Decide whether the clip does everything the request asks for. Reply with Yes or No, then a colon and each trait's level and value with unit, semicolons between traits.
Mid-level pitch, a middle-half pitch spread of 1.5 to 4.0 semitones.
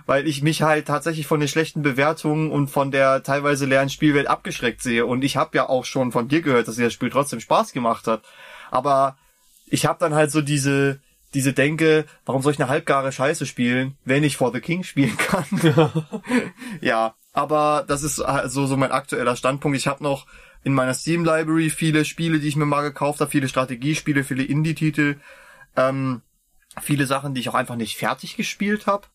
Yes: medium, 145 Hz; average, 2.8 semitones